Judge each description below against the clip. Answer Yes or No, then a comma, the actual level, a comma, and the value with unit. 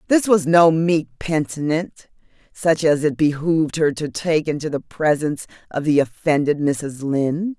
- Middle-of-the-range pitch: Yes, medium, 155 Hz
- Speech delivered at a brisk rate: No, average, 160 wpm